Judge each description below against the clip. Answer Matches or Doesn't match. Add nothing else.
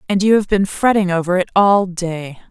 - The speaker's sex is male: Doesn't match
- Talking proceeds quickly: Matches